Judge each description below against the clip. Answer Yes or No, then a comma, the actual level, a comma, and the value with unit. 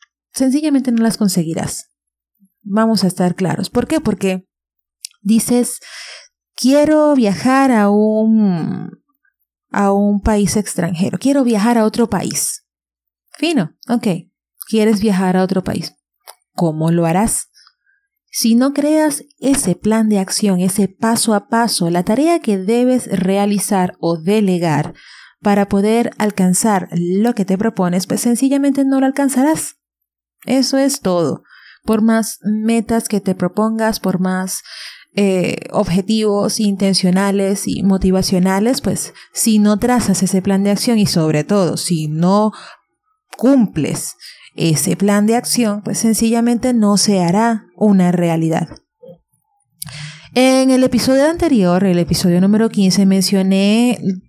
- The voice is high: Yes, high, 205 Hz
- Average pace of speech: No, slow, 125 wpm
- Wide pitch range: No, average, 4.0 semitones